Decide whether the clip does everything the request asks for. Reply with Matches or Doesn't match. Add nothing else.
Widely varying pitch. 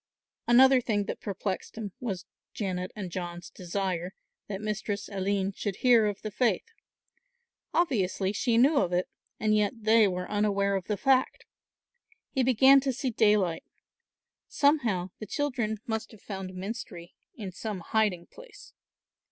Doesn't match